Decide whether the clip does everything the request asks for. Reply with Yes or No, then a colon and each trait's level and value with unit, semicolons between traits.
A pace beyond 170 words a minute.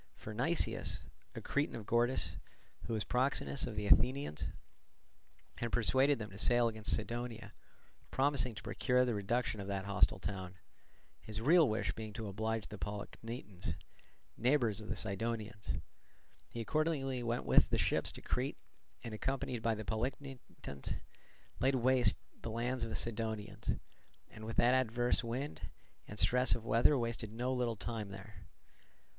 No: average, 150 wpm